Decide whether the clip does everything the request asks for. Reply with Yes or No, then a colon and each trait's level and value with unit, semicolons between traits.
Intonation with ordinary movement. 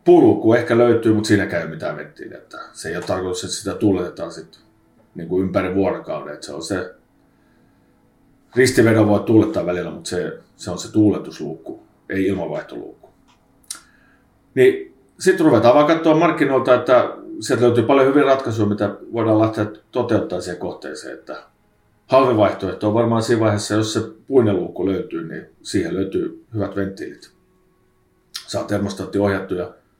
No: wide, 5.7 semitones